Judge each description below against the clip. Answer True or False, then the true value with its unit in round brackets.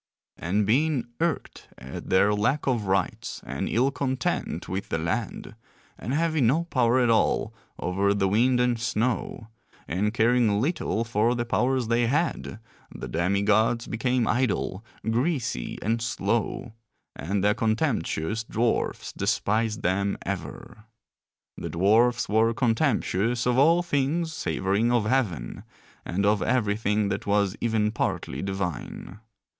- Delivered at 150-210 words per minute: False (135 wpm)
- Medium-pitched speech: False (115 Hz)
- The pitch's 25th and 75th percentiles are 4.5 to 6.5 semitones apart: False (3.6 semitones)